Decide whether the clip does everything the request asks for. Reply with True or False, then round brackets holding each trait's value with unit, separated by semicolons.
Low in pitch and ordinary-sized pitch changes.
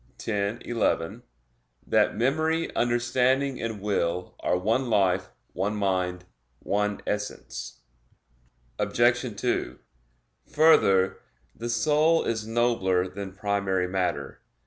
True (105 Hz; 4.3 semitones)